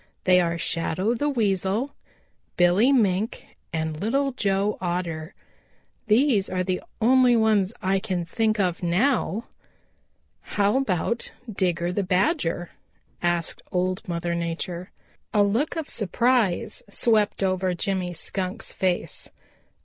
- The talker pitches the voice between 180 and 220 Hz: Yes, high, 190 Hz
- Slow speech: Yes, slow, 120 wpm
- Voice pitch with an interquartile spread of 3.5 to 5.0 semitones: Yes, average, 4.0 semitones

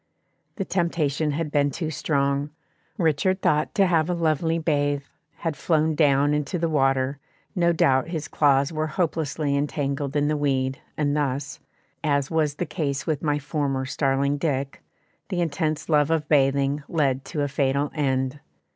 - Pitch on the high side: No, medium, 145 Hz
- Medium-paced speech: Yes, average, 160 wpm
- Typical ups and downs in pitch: No, narrow, 2.3 semitones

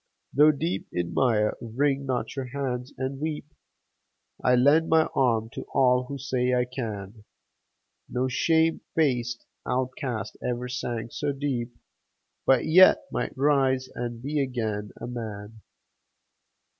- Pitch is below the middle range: Yes, low, 125 Hz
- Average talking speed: No, slow, 130 wpm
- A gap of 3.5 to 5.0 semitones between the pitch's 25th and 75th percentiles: No, average, 2.8 semitones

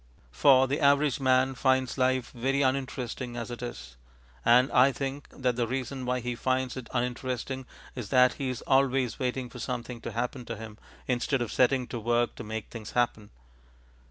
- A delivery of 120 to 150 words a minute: No, average, 185 wpm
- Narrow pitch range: Yes, narrow, 1.6 semitones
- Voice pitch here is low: Yes, low, 125 Hz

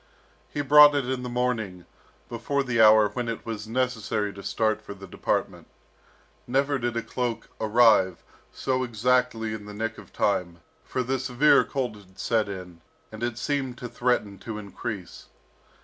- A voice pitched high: No, low, 115 Hz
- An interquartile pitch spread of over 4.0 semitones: No, average, 3.3 semitones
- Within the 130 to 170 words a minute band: Yes, average, 165 wpm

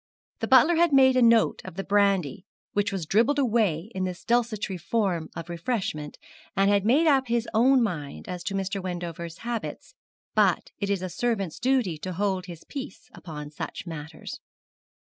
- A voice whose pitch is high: Yes, high, 195 Hz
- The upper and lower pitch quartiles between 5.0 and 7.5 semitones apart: Yes, average, 5.3 semitones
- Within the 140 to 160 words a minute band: No, average, 175 wpm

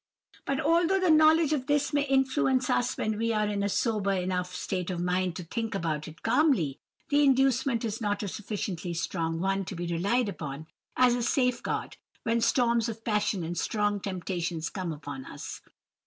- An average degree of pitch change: No, wide, 6.0 semitones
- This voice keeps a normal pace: Yes, average, 185 wpm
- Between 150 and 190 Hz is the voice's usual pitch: No, high, 210 Hz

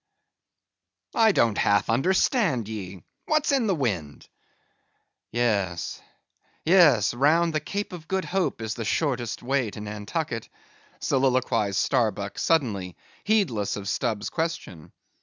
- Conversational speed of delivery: No, slow, 120 wpm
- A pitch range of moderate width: No, wide, 8.3 semitones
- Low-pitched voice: Yes, low, 120 Hz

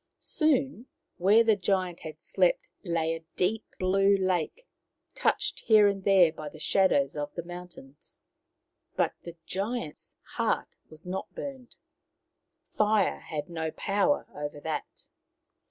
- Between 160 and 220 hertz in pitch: Yes, medium, 185 Hz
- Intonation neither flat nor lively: Yes, average, 4.9 semitones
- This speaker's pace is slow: Yes, slow, 130 wpm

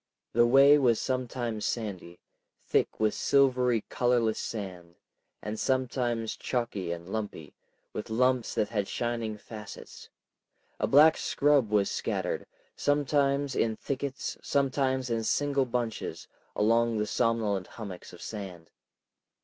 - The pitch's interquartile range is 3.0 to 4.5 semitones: Yes, average, 3.6 semitones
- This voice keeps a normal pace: No, slow, 120 wpm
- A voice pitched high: No, low, 115 Hz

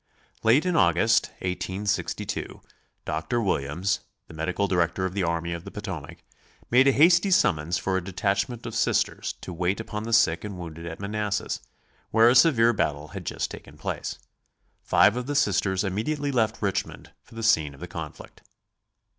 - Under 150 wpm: No, average, 170 wpm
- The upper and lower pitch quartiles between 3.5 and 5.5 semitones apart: Yes, average, 4.9 semitones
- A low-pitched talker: Yes, low, 100 Hz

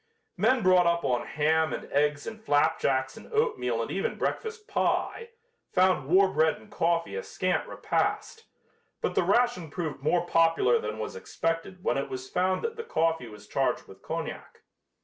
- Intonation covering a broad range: Yes, wide, 6.7 semitones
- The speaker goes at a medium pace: Yes, average, 170 wpm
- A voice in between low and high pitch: Yes, medium, 170 Hz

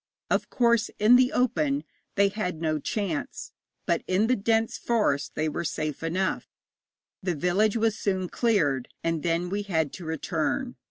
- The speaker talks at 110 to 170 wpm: Yes, average, 160 wpm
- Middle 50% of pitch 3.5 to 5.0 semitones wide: No, wide, 5.6 semitones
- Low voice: No, high, 190 Hz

